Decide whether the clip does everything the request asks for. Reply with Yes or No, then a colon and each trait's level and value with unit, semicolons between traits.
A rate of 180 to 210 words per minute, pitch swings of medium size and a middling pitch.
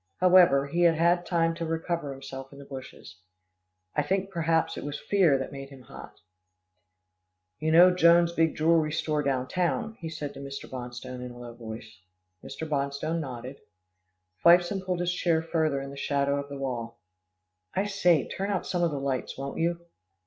Yes: average, 185 wpm; average, 3.9 semitones; medium, 155 Hz